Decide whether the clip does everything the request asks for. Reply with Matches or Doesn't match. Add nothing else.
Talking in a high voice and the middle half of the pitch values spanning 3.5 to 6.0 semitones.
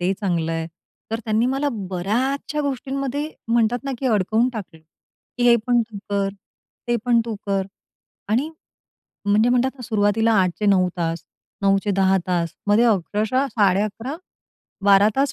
Matches